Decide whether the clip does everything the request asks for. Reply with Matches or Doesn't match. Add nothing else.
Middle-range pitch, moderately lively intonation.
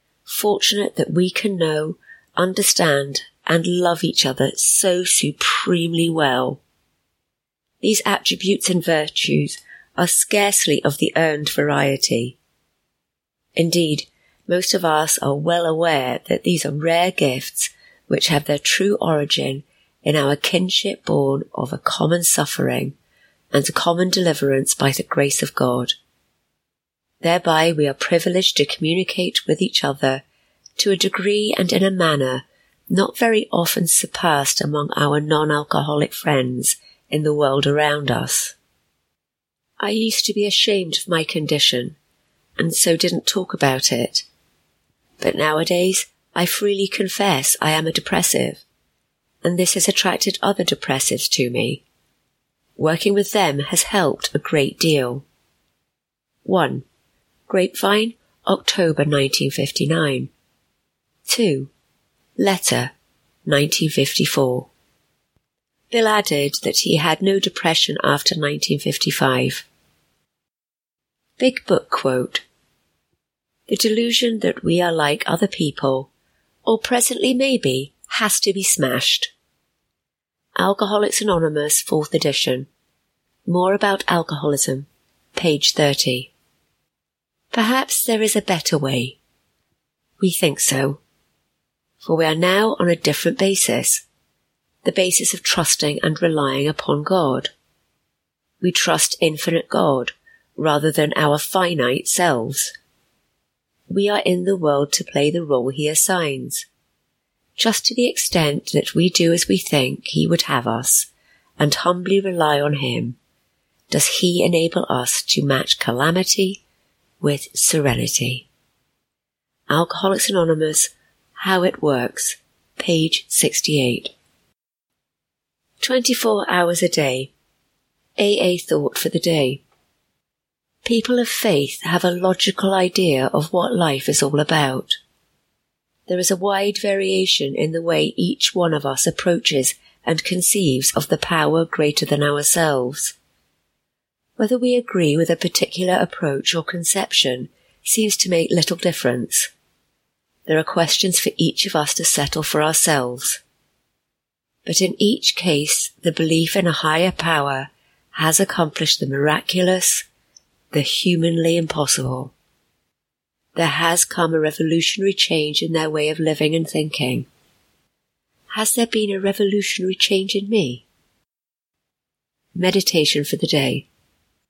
Matches